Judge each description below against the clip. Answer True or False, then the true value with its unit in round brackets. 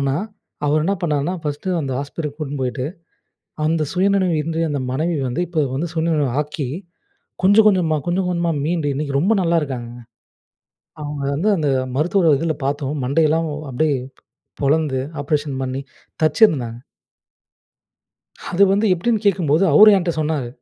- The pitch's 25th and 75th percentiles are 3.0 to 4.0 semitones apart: True (3.6 semitones)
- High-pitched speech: False (155 Hz)